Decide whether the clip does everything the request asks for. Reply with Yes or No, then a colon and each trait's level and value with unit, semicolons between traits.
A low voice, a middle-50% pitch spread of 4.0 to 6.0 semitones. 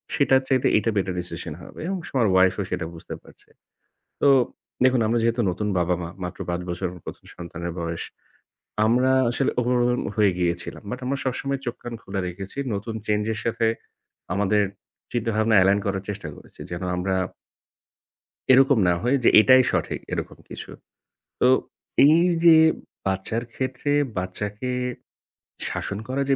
Yes: low, 105 Hz; average, 5.3 semitones